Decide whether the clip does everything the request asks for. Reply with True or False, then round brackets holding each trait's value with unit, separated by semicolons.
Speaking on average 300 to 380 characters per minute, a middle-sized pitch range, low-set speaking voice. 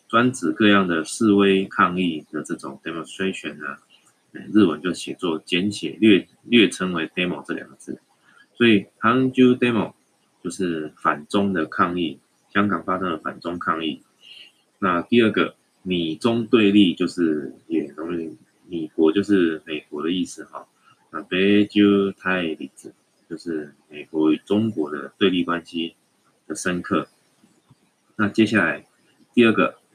False (255 characters per minute; 3.4 semitones; 95 Hz)